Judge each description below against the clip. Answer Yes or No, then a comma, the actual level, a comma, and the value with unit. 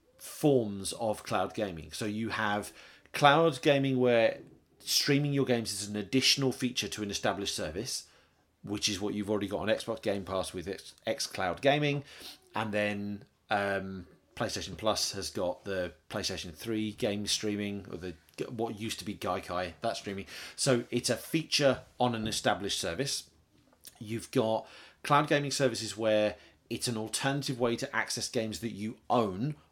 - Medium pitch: No, low, 110 Hz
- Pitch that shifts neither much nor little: Yes, average, 3.7 semitones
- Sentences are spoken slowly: No, average, 160 wpm